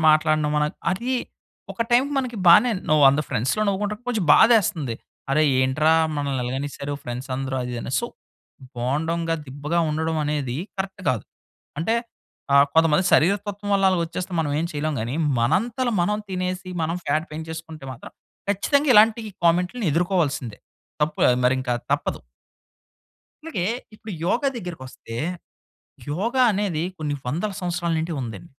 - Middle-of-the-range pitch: Yes, medium, 160 Hz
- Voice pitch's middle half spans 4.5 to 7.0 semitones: Yes, wide, 5.5 semitones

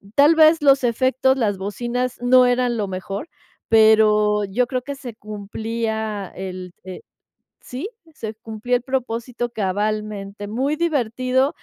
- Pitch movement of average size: Yes, average, 3.5 semitones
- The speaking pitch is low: No, high, 230 Hz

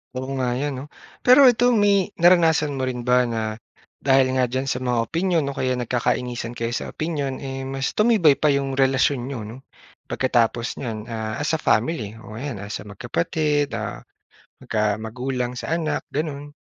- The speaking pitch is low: Yes, low, 130 Hz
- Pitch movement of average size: Yes, average, 3.7 semitones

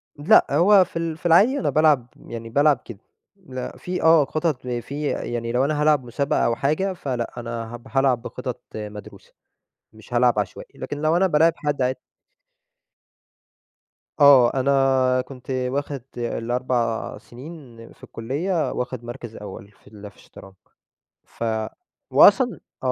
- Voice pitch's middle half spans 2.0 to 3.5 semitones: No, average, 4.3 semitones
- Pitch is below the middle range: Yes, low, 130 Hz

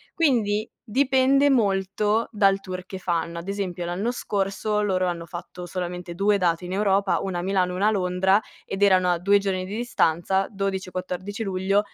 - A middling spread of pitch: No, narrow, 2.3 semitones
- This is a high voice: Yes, high, 195 Hz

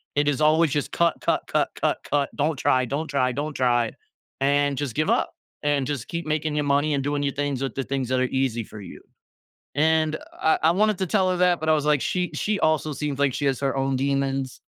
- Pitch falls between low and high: Yes, medium, 145 Hz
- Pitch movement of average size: No, narrow, 2.3 semitones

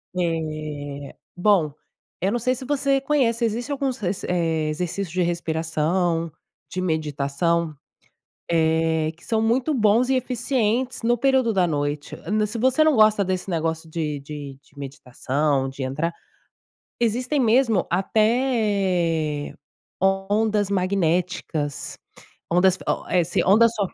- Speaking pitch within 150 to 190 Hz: Yes, medium, 185 Hz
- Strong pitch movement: Yes, wide, 6.1 semitones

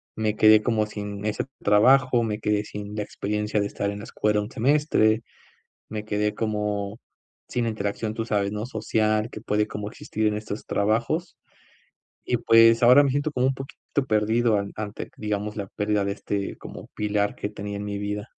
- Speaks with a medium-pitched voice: No, low, 105 Hz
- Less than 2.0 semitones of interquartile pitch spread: Yes, narrow, 1.5 semitones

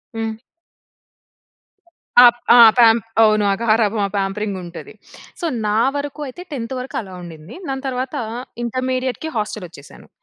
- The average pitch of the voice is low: No, high, 225 Hz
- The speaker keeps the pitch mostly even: No, average, 3.7 semitones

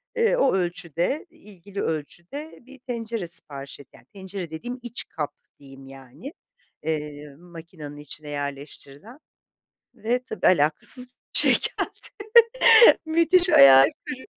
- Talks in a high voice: No, medium, 175 Hz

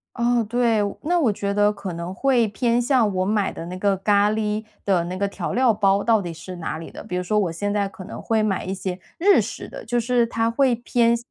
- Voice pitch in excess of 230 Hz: No, high, 210 Hz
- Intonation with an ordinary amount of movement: Yes, average, 3.7 semitones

